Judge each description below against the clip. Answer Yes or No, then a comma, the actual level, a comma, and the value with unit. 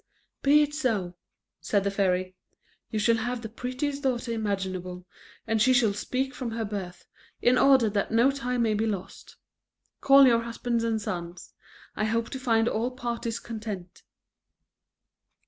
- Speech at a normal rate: Yes, average, 155 wpm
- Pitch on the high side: Yes, high, 230 Hz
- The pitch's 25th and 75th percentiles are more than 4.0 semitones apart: No, average, 3.7 semitones